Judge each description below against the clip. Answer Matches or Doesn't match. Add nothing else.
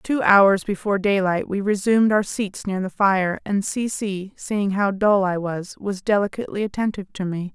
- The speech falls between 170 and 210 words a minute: Matches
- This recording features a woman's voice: Matches